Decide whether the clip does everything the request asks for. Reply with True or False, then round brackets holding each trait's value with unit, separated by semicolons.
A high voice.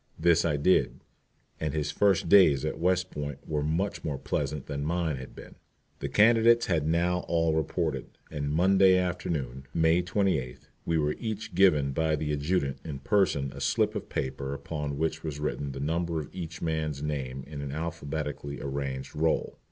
False (80 Hz)